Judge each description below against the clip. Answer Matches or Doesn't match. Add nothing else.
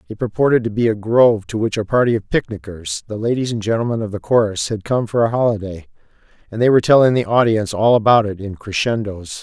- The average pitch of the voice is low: Matches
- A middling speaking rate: Doesn't match